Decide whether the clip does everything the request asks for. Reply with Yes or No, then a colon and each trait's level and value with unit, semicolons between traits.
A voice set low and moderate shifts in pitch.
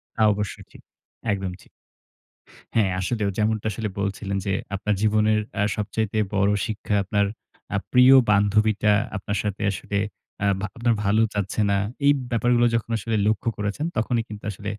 No: low, 105 Hz; narrow, 1.6 semitones